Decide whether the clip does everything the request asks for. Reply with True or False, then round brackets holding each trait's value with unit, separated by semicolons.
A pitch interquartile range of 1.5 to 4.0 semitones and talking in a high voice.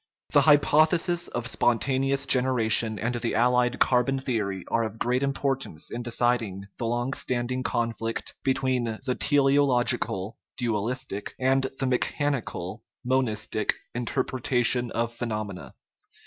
False (2.5 semitones; 125 Hz)